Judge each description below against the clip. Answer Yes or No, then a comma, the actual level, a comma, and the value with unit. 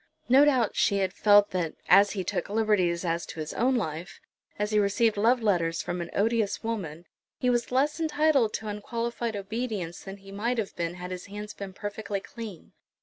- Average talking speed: Yes, average, 195 wpm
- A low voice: No, high, 205 Hz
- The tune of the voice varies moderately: Yes, average, 4.0 semitones